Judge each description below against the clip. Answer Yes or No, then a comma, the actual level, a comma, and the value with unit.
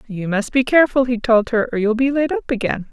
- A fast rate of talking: Yes, fast, 265 wpm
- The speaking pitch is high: Yes, high, 235 Hz